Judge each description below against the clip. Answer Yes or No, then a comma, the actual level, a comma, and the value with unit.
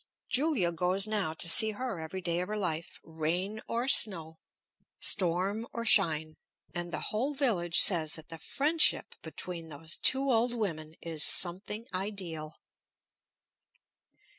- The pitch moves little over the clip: No, average, 5.1 semitones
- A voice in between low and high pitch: Yes, medium, 180 Hz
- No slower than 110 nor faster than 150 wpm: Yes, average, 140 wpm